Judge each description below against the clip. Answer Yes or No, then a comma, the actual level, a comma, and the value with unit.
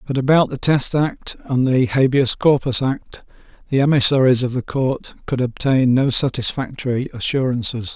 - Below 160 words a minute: Yes, average, 150 wpm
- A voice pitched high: No, low, 135 Hz